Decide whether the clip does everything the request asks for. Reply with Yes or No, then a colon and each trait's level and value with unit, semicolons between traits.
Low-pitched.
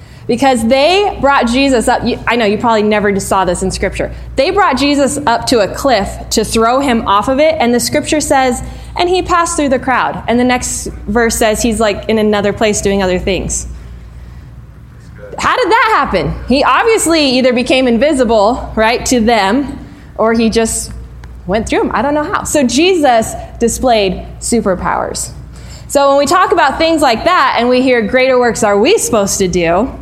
No: high, 240 Hz